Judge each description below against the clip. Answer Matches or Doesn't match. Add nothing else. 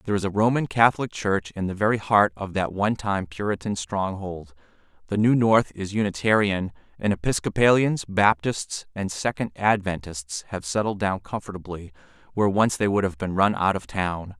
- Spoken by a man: Matches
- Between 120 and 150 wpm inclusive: Doesn't match